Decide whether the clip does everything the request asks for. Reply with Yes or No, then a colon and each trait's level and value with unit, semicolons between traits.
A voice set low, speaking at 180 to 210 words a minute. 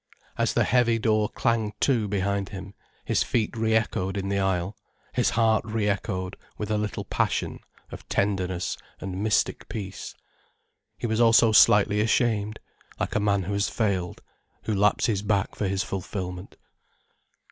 No: low, 105 Hz; average, 155 wpm